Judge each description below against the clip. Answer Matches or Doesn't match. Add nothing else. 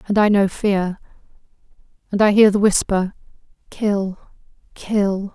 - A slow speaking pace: Matches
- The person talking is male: Doesn't match